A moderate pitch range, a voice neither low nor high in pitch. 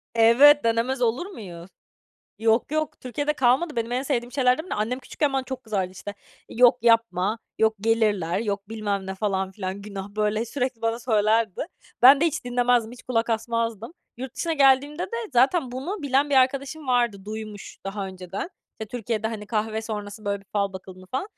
No: average, 4.0 semitones; high, 230 Hz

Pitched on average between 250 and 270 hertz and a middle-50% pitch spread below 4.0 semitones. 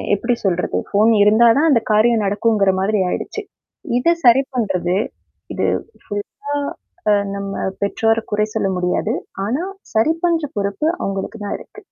No: high, 220 Hz; average, 3.6 semitones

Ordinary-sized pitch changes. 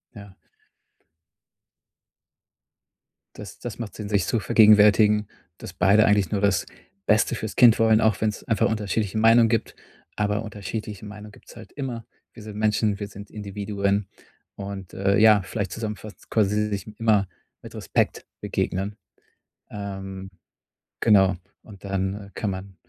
No: narrow, 1.7 semitones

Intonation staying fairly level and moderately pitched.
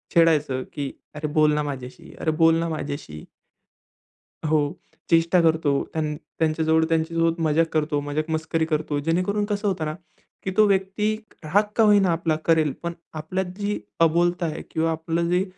Yes: narrow, 2.0 semitones; medium, 160 Hz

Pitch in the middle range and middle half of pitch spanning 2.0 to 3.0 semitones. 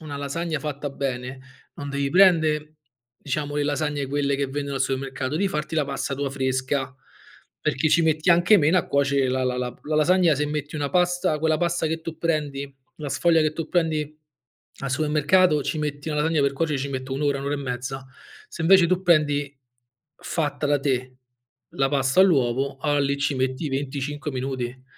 Yes: medium, 145 Hz; narrow, 2.4 semitones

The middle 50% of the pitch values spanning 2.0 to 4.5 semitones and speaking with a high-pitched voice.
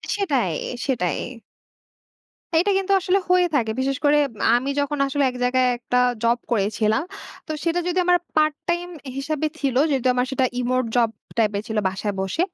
No: average, 5.1 semitones; very high, 265 Hz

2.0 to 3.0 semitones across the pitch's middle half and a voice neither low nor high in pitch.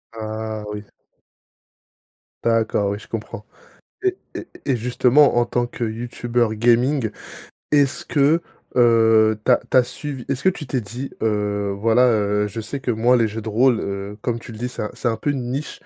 No: average, 2.7 semitones; low, 115 Hz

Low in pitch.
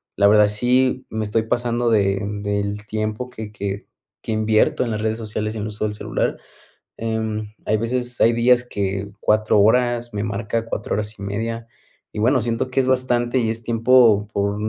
Yes: low, 110 Hz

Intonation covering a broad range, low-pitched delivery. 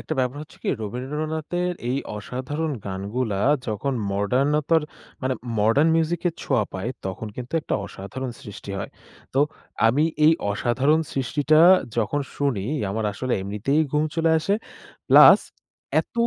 Yes: wide, 6.3 semitones; low, 130 Hz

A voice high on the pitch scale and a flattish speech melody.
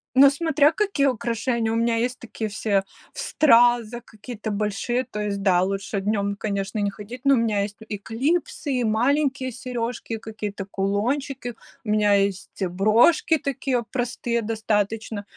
No: high, 225 Hz; average, 3.6 semitones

